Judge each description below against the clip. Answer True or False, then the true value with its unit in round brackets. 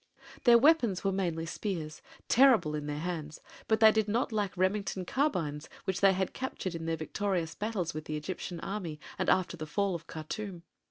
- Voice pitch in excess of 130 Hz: True (185 Hz)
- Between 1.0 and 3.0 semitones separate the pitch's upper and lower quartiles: False (4.5 semitones)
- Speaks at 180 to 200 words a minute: True (185 wpm)